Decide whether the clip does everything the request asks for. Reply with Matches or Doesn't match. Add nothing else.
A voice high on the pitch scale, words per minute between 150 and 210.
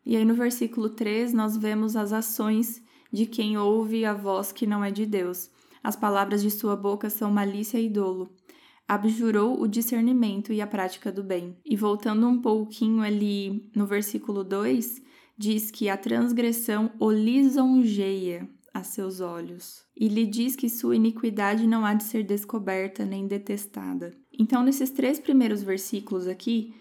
Matches